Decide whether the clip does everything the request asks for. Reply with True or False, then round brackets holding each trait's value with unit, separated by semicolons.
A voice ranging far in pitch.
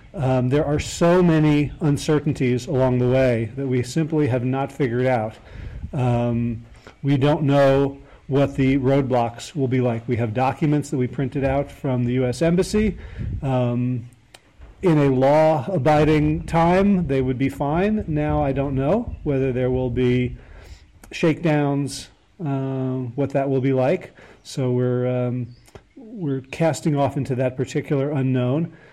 False (3.1 semitones)